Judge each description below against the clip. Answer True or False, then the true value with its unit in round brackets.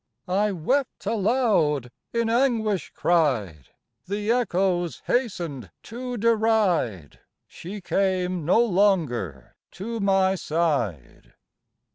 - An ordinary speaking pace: False (90 wpm)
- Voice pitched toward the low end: False (190 Hz)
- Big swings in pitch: True (6.6 semitones)